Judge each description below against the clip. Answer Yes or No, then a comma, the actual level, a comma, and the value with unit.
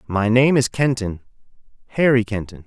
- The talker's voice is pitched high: No, low, 115 Hz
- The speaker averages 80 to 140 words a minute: Yes, slow, 135 wpm